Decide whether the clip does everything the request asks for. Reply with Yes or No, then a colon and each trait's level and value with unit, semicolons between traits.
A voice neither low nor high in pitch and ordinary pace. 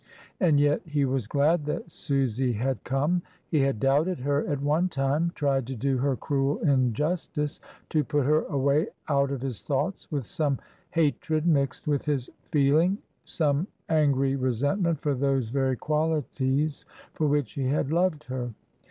Yes: medium, 145 Hz; average, 160 wpm